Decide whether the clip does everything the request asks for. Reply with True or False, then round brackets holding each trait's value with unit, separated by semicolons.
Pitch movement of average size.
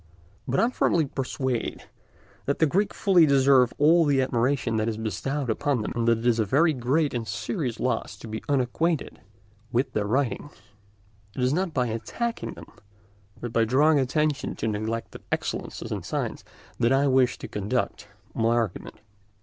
True (4.0 semitones)